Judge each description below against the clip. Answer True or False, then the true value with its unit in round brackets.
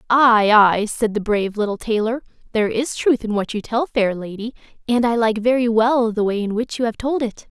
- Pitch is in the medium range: False (230 Hz)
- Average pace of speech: False (230 wpm)